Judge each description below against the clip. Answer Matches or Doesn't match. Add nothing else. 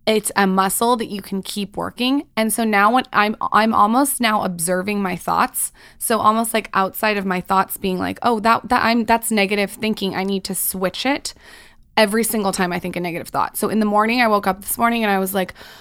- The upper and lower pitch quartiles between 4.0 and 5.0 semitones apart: Doesn't match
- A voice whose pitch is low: Doesn't match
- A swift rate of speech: Matches